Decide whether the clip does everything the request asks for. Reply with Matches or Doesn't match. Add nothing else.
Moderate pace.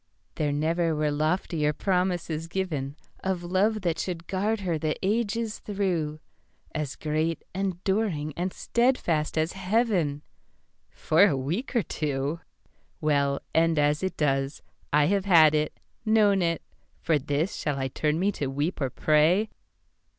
Doesn't match